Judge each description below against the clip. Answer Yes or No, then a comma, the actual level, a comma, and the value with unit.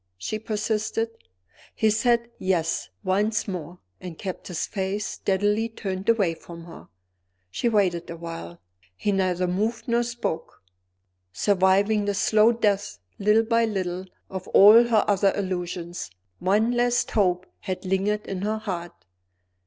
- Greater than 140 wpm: No, slow, 135 wpm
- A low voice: No, high, 200 Hz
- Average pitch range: Yes, average, 3.1 semitones